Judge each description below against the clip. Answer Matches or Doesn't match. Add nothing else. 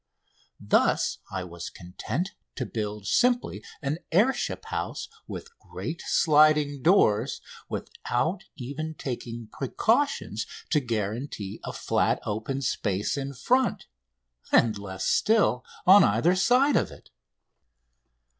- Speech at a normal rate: Doesn't match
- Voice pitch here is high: Doesn't match